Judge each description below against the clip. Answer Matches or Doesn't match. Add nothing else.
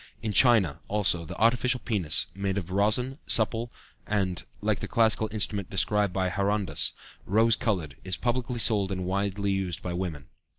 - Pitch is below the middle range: Matches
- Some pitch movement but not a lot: Matches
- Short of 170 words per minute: Matches